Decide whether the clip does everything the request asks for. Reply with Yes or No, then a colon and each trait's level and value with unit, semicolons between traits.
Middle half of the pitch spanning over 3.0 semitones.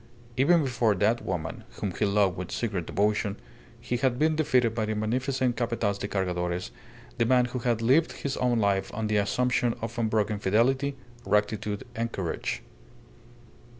Yes: average, 3.6 semitones